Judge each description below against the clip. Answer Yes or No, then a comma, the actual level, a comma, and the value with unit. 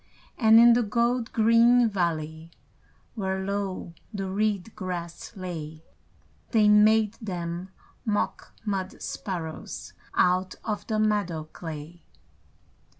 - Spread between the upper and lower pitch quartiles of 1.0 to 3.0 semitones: No, average, 3.9 semitones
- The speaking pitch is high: Yes, high, 195 Hz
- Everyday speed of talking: No, slow, 105 wpm